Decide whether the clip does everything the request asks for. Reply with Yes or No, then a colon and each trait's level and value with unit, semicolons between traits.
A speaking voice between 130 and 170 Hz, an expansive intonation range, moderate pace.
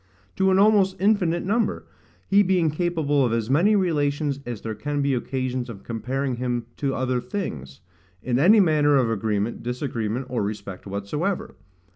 Yes: low, 135 Hz; wide, 6.7 semitones; average, 160 wpm